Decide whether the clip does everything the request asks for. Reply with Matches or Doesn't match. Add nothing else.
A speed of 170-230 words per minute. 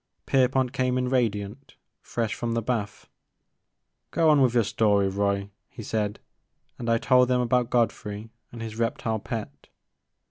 Doesn't match